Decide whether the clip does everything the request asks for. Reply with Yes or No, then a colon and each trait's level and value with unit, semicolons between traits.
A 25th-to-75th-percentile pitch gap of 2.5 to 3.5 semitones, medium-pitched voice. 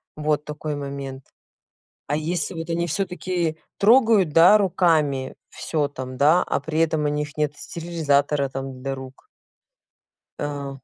Yes: average, 3.2 semitones; medium, 150 Hz